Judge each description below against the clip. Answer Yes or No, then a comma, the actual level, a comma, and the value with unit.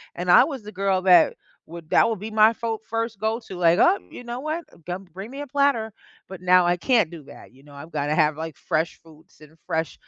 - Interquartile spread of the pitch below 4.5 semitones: No, wide, 5.6 semitones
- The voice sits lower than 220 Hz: Yes, high, 190 Hz